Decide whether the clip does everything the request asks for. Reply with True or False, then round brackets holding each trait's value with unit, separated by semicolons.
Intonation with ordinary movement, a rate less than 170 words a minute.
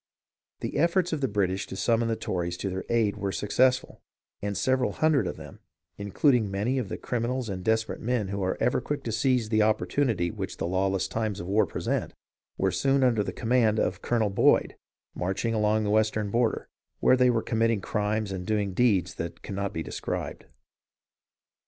False (3.8 semitones; 185 wpm)